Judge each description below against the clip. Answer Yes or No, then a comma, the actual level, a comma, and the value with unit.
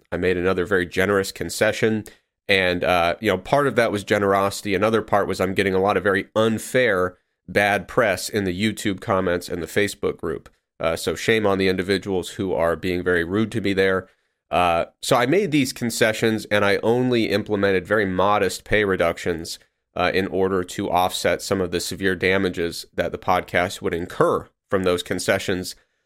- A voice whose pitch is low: Yes, very low, 95 Hz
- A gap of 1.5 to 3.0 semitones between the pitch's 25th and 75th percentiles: Yes, narrow, 2.5 semitones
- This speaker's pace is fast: No, average, 185 wpm